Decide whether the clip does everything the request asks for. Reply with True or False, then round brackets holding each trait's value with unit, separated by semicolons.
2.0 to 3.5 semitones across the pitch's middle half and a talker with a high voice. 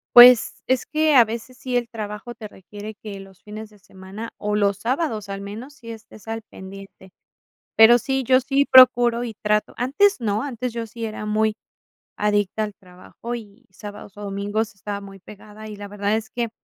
True (2.8 semitones; 215 Hz)